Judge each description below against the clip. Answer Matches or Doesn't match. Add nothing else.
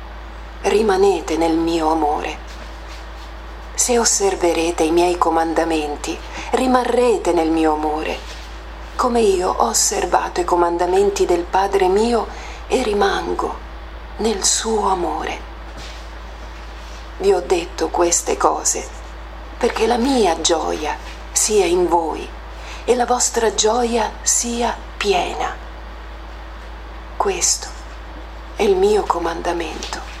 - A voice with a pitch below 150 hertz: Doesn't match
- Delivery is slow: Matches